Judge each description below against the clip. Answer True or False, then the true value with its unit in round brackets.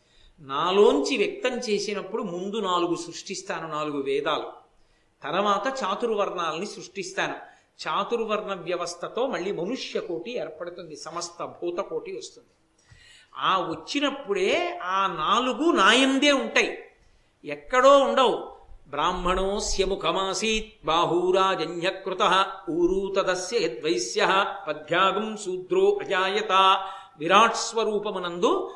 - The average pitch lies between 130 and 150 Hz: False (195 Hz)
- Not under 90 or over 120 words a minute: False (75 wpm)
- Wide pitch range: True (6.8 semitones)